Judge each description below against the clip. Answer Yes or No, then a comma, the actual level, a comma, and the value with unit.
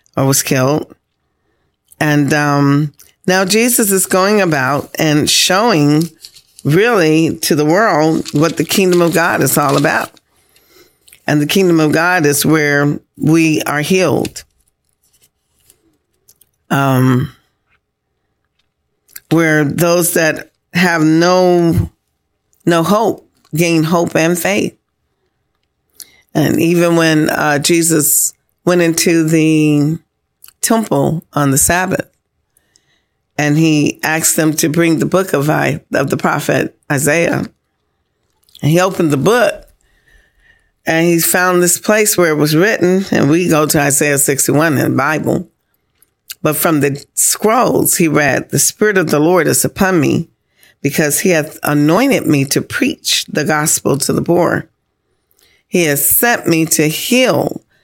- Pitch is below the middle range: No, medium, 160 Hz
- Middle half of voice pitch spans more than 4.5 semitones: No, average, 2.8 semitones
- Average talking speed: No, slow, 130 wpm